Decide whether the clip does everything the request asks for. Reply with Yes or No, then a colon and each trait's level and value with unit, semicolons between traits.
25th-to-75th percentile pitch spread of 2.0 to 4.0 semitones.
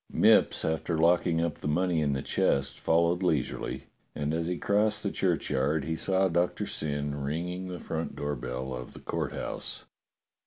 Yes: average, 3.5 semitones